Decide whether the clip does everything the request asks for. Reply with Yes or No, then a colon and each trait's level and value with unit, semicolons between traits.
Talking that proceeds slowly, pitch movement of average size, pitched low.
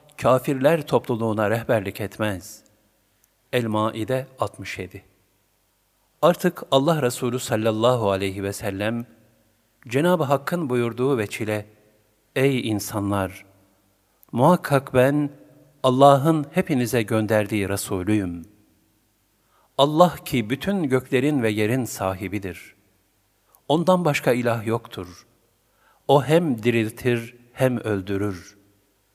Yes: slow, 85 wpm; average, 4.2 semitones; low, 115 Hz